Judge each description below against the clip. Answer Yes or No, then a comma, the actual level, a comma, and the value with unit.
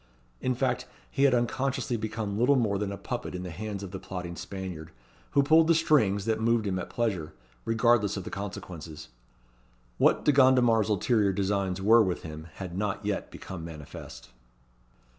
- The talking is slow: No, average, 175 wpm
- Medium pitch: No, low, 105 Hz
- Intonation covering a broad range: No, average, 4.2 semitones